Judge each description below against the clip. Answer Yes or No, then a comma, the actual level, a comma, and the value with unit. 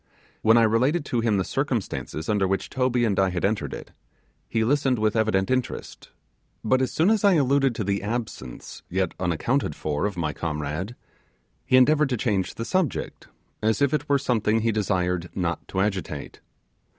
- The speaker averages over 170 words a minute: Yes, average, 180 wpm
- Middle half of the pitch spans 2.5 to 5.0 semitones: No, wide, 5.4 semitones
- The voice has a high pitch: No, low, 110 Hz